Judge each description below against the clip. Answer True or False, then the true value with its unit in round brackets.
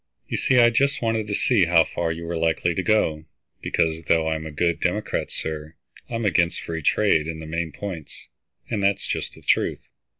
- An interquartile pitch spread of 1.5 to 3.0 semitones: False (4.3 semitones)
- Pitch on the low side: True (85 Hz)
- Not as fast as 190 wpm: False (200 wpm)